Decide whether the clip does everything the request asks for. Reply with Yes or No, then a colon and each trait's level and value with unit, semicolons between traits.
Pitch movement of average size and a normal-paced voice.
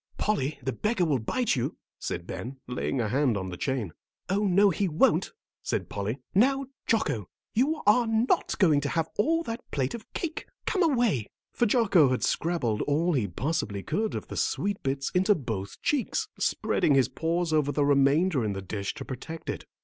No: wide, 8.6 semitones; average, 190 wpm